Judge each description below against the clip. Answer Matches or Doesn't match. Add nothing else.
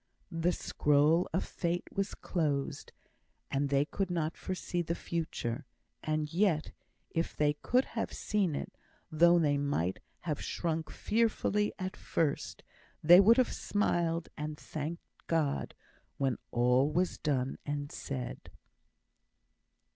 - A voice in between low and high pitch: Matches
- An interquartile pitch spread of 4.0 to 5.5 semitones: Doesn't match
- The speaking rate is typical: Doesn't match